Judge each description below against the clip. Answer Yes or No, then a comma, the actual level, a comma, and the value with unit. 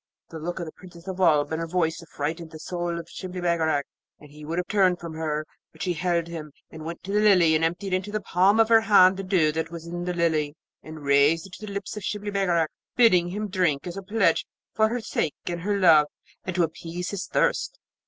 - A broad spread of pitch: No, average, 3.0 semitones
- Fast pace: Yes, fast, 240 wpm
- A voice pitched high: No, medium, 175 Hz